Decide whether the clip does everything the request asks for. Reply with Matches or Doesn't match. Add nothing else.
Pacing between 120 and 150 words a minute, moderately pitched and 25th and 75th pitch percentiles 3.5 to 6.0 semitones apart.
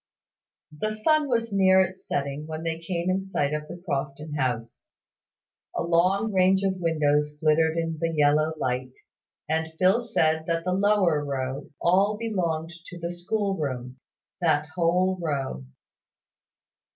Matches